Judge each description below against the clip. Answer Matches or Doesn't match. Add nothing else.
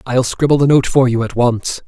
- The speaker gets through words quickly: Matches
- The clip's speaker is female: Doesn't match